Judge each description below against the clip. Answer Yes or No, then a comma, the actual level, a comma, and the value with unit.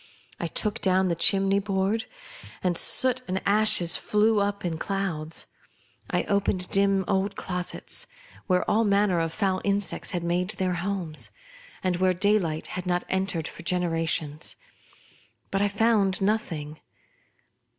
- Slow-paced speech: Yes, slow, 120 wpm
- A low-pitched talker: No, high, 190 Hz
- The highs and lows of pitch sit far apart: No, narrow, 2.5 semitones